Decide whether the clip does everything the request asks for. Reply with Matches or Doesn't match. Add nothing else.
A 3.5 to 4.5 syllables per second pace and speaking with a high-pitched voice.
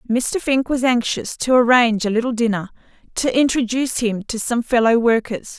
Doesn't match